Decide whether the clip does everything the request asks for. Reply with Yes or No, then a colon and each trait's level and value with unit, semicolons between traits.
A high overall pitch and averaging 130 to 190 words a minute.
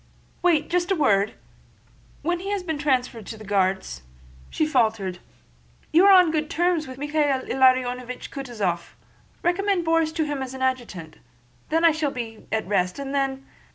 Yes: very high, 270 Hz; average, 155 wpm